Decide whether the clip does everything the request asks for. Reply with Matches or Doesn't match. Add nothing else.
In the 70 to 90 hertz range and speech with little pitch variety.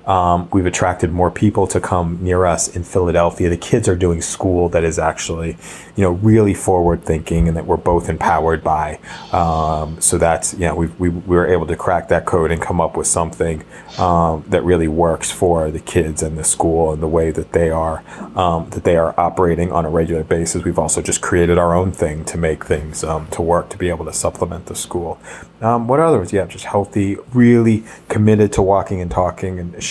Matches